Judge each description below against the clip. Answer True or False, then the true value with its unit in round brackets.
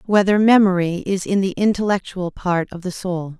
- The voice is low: False (190 Hz)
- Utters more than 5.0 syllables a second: False (4.9 syllables/s)